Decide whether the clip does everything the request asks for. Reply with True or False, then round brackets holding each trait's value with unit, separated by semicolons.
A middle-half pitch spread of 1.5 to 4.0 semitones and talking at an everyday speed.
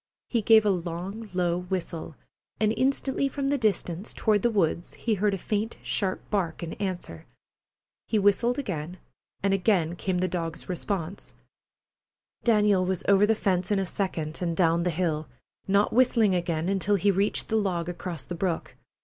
True (3.3 semitones; 170 wpm)